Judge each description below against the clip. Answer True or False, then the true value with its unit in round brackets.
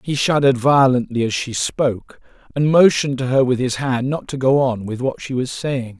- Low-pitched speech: True (130 Hz)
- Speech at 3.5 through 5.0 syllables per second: False (5.3 syllables/s)